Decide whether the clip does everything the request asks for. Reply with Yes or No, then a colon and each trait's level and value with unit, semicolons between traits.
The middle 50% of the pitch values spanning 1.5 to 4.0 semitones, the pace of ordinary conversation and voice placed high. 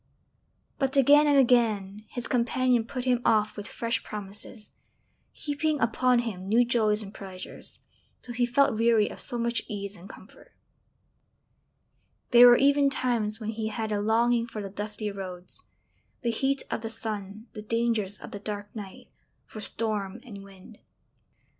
Yes: average, 2.8 semitones; average, 160 wpm; high, 225 Hz